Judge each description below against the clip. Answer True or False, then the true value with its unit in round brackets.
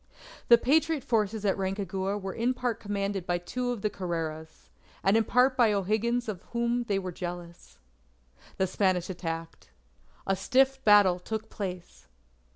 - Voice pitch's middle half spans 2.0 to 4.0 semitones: False (4.5 semitones)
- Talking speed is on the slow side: False (155 wpm)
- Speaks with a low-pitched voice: False (200 Hz)